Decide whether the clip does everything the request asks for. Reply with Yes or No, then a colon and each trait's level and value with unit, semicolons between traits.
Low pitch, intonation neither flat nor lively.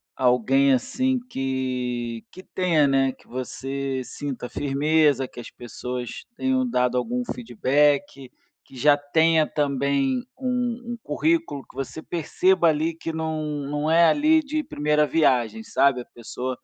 No: medium, 145 Hz; average, 4.2 semitones